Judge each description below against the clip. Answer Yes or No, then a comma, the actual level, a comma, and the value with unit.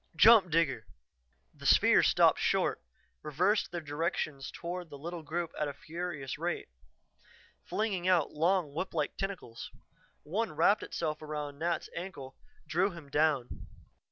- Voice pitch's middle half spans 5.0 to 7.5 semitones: No, average, 3.3 semitones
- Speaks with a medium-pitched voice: Yes, medium, 165 Hz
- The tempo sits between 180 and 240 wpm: No, slow, 135 wpm